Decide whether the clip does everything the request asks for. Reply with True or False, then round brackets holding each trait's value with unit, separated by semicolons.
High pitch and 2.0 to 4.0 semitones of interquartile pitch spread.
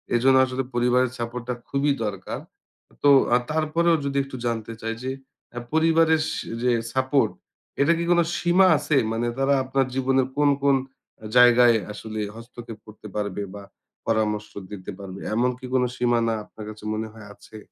False (125 Hz; 3.6 semitones)